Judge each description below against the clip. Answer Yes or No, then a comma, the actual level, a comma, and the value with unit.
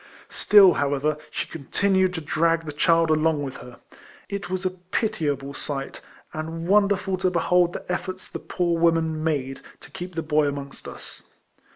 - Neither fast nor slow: Yes, average, 165 wpm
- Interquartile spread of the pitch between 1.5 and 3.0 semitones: No, average, 3.4 semitones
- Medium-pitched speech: Yes, medium, 165 Hz